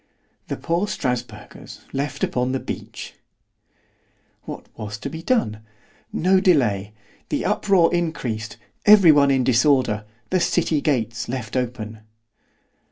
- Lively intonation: Yes, wide, 6.8 semitones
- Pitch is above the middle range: No, low, 130 Hz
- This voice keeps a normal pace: No, slow, 100 wpm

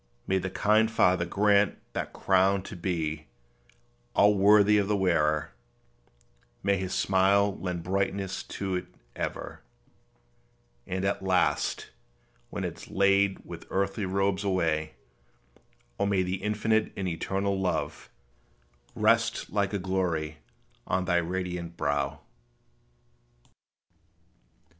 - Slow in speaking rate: Yes, slow, 115 wpm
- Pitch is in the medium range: No, very low, 95 Hz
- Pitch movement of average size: No, narrow, 1.9 semitones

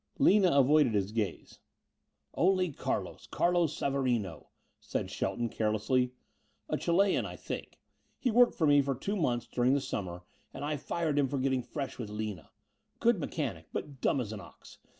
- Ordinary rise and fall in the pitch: No, wide, 6.3 semitones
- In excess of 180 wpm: No, average, 165 wpm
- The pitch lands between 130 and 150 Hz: Yes, low, 135 Hz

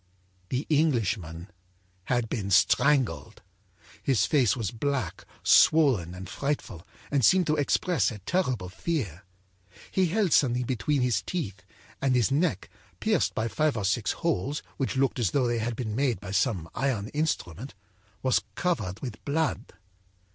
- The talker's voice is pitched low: Yes, low, 125 Hz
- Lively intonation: Yes, wide, 6.1 semitones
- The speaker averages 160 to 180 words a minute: No, average, 145 wpm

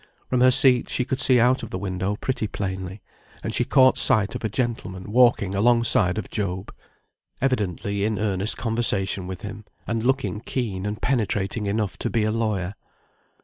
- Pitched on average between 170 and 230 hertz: No, low, 105 Hz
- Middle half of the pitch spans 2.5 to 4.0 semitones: Yes, average, 3.7 semitones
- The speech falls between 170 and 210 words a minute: Yes, average, 175 wpm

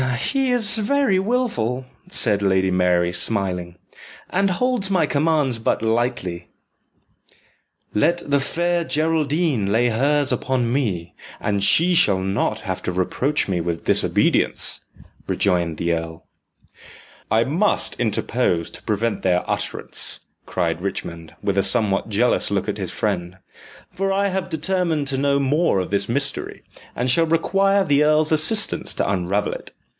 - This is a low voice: Yes, low, 125 Hz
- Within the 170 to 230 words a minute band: No, average, 140 wpm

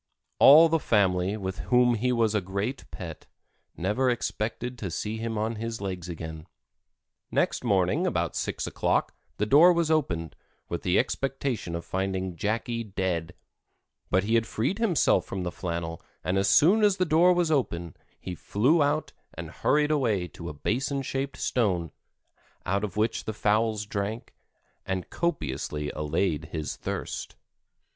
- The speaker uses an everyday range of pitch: No, wide, 6.5 semitones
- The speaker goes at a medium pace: Yes, average, 155 wpm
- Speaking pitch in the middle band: No, low, 105 Hz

